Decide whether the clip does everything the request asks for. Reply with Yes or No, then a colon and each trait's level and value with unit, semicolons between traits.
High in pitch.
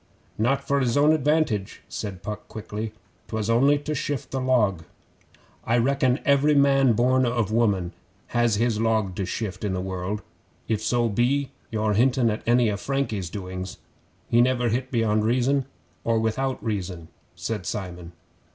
No: low, 115 Hz